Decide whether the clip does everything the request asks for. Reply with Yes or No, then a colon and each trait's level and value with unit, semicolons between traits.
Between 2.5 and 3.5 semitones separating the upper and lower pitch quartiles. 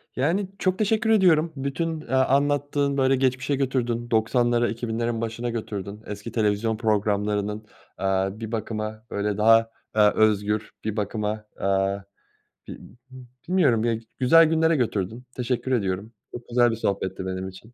No: average, 3.9 semitones